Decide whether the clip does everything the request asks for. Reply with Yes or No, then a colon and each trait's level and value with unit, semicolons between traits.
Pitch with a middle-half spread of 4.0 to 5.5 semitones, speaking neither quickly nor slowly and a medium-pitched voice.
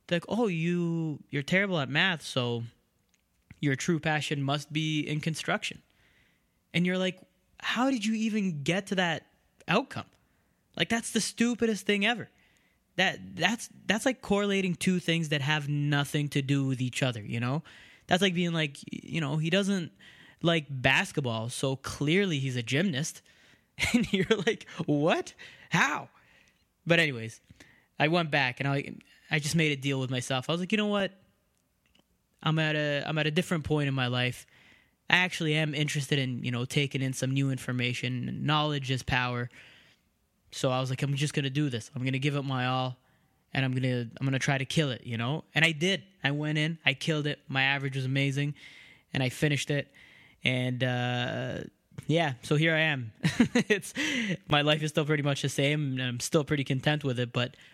Yes: average, 4.5 semitones; average, 190 wpm; medium, 150 Hz